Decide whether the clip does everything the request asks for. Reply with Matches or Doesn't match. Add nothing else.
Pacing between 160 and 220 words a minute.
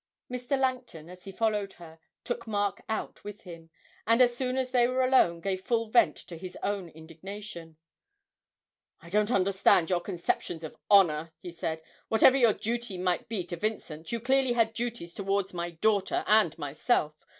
Matches